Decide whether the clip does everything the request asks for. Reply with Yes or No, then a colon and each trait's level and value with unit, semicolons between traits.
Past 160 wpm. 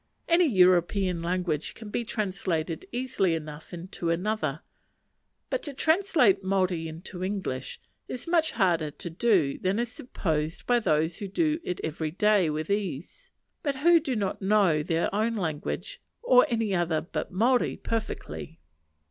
No: average, 150 wpm